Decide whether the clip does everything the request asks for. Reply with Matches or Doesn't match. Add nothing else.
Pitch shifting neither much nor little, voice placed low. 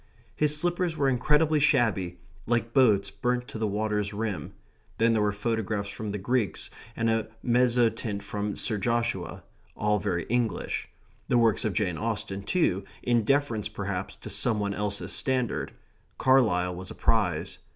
Matches